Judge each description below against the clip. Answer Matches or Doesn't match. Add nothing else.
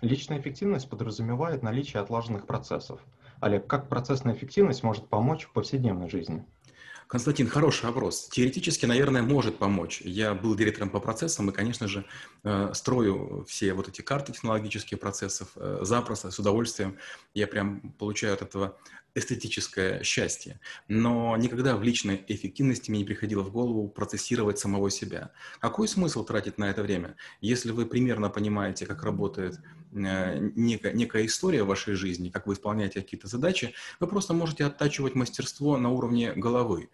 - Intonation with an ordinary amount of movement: Matches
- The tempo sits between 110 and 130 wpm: Doesn't match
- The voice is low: Matches